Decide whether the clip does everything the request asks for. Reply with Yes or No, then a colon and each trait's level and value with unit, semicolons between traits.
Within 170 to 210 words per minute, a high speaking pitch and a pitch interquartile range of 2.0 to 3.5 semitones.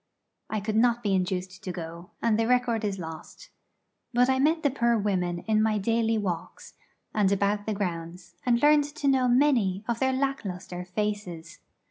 No: average, 180 wpm; high, 215 Hz; average, 5.0 semitones